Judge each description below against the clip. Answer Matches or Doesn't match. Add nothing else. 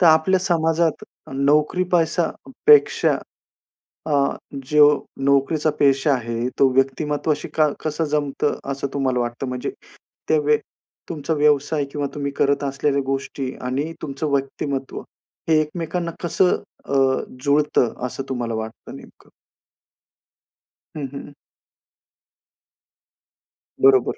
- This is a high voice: Doesn't match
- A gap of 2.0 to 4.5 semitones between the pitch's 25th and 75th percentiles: Matches